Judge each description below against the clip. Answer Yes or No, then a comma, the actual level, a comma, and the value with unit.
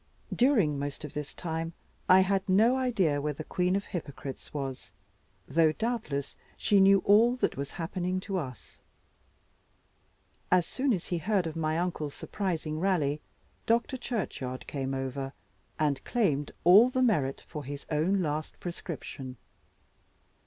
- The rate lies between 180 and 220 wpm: No, average, 145 wpm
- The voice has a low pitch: No, medium, 165 Hz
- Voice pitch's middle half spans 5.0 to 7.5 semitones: Yes, wide, 5.4 semitones